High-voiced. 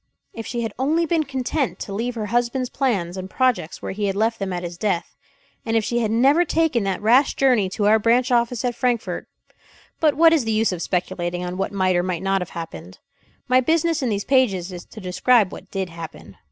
Yes: high, 225 Hz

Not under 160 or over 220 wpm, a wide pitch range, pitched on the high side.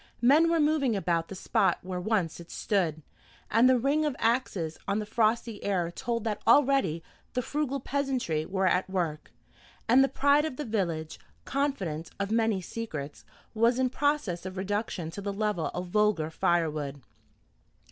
Yes: average, 165 wpm; wide, 6.6 semitones; high, 210 Hz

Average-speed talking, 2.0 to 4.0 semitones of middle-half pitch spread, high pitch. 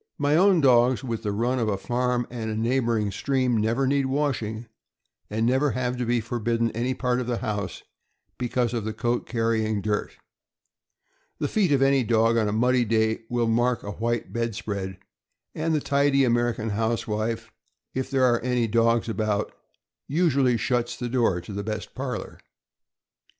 No: average, 170 wpm; narrow, 2.5 semitones; low, 120 Hz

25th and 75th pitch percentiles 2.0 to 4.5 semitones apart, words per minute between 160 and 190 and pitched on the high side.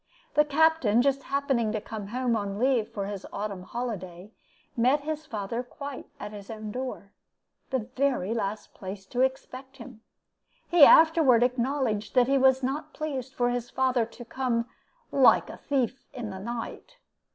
Yes: average, 4.0 semitones; average, 165 wpm; high, 245 Hz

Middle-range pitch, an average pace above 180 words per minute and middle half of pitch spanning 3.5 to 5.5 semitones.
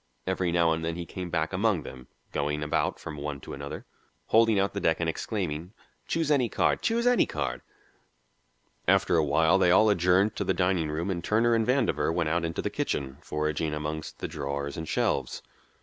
No: very low, 85 Hz; average, 195 wpm; average, 4.3 semitones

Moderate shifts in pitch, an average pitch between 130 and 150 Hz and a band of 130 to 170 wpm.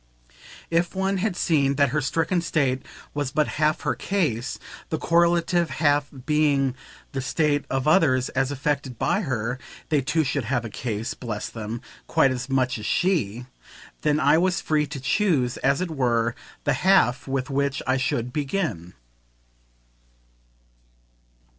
Yes: average, 3.9 semitones; medium, 140 Hz; average, 150 wpm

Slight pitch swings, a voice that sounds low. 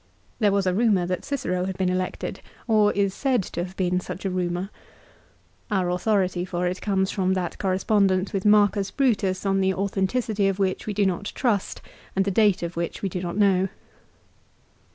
No: narrow, 1.9 semitones; high, 190 Hz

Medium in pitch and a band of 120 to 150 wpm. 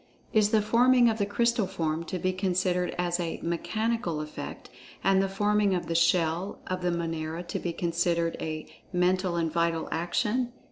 No: medium, 180 Hz; average, 175 wpm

